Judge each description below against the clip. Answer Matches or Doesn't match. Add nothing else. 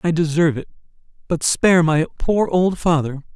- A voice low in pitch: Doesn't match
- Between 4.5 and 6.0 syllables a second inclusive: Matches